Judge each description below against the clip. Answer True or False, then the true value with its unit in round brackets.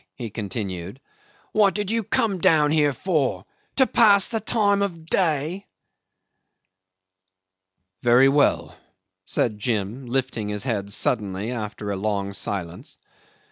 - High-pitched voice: False (130 Hz)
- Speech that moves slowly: True (120 wpm)